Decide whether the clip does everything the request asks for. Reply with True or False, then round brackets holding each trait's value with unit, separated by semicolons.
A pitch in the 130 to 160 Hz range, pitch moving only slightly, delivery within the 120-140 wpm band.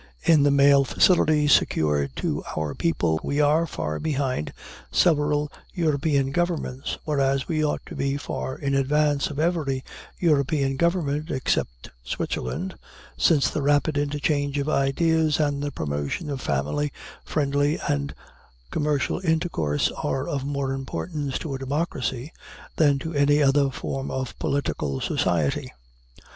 True (140 Hz; 2.2 semitones; 135 wpm)